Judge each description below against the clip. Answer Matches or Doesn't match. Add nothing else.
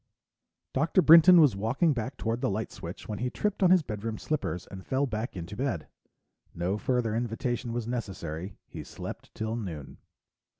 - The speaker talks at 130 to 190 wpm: Matches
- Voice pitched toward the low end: Matches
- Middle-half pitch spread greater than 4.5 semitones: Matches